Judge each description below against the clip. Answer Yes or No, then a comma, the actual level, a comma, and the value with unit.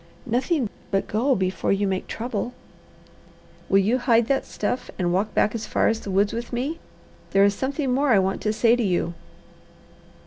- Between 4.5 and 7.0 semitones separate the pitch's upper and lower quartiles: No, average, 4.0 semitones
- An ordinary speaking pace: Yes, average, 185 wpm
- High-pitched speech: Yes, high, 225 Hz